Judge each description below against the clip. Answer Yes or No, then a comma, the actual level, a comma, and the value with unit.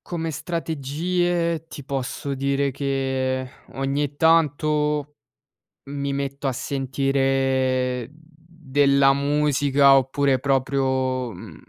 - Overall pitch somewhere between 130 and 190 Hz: Yes, medium, 140 Hz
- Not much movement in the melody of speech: Yes, narrow, 2.0 semitones